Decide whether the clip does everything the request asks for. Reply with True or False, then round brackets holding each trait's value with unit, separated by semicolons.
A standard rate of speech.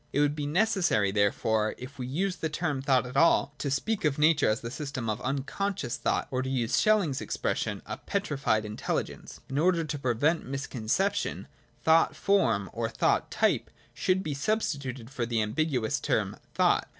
True (175 wpm)